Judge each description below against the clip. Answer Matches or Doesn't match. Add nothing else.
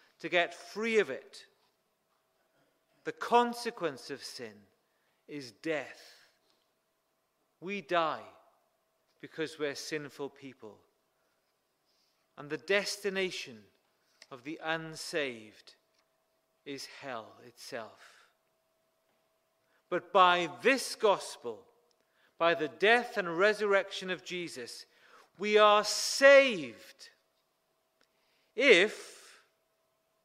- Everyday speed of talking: Doesn't match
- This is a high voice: Doesn't match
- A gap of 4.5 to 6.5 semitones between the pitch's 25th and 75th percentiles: Matches